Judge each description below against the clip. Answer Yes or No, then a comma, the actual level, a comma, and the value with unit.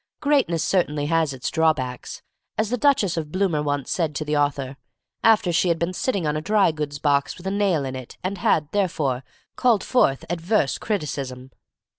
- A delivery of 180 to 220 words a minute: Yes, average, 185 wpm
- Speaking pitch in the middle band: Yes, medium, 160 Hz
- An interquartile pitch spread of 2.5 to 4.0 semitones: No, average, 5.3 semitones